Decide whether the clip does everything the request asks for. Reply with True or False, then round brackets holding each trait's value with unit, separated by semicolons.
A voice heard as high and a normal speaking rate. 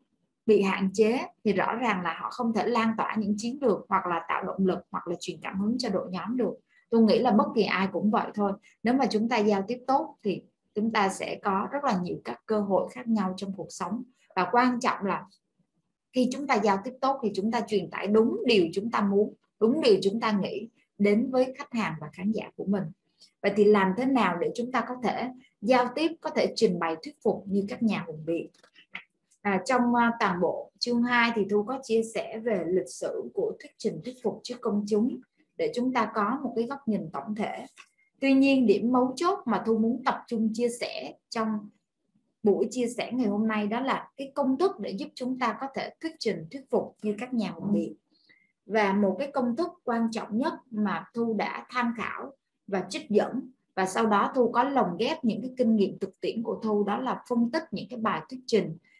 True (225 Hz; 235 wpm)